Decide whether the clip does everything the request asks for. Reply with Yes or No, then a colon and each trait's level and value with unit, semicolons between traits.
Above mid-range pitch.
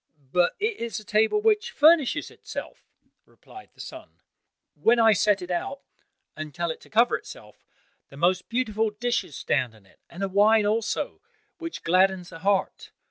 Yes: high, 210 Hz